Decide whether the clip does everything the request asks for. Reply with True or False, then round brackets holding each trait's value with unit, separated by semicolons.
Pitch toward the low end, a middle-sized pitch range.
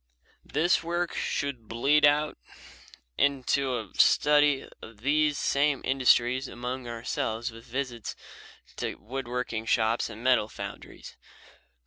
True (130 Hz; 3.4 semitones)